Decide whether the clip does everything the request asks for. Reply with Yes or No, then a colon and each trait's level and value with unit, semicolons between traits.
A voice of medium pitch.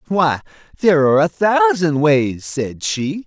Yes: medium, 165 Hz